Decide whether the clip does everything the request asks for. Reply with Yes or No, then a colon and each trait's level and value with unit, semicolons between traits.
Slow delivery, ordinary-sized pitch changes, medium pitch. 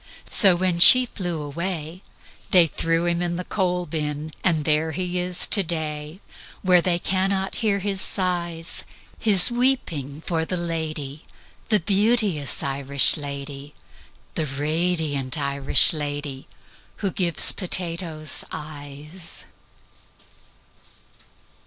Yes: slow, 115 wpm; average, 3.7 semitones; medium, 165 Hz